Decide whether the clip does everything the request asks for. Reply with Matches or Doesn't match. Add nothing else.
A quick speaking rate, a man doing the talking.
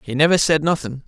Matches